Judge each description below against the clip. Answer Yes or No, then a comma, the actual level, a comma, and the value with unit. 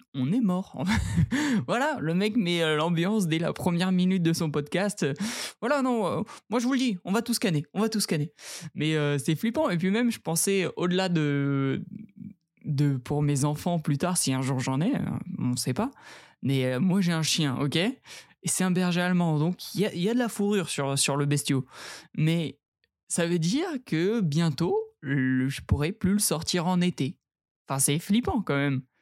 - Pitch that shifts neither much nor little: No, wide, 5.8 semitones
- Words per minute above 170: Yes, average, 205 wpm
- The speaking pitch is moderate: Yes, medium, 175 Hz